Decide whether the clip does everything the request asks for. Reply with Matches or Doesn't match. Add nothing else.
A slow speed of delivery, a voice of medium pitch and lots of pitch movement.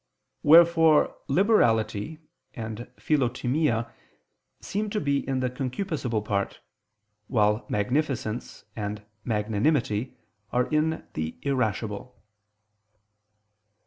Doesn't match